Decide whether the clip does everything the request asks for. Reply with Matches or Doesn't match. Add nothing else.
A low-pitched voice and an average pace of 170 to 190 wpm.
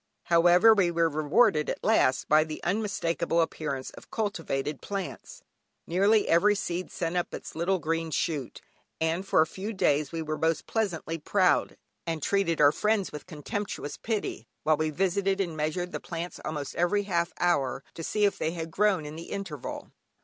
Doesn't match